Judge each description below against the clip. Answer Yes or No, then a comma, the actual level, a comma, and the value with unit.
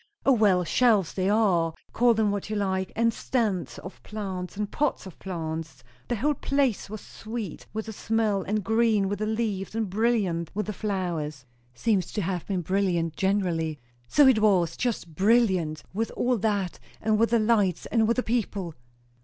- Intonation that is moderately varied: Yes, average, 3.5 semitones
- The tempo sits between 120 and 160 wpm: No, average, 185 wpm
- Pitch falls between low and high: No, high, 205 Hz